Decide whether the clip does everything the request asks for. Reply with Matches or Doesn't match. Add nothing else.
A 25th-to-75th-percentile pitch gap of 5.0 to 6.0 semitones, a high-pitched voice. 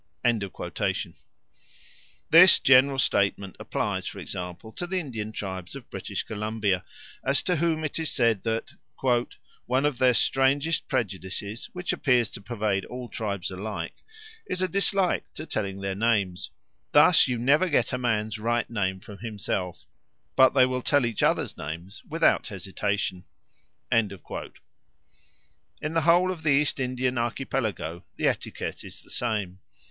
Doesn't match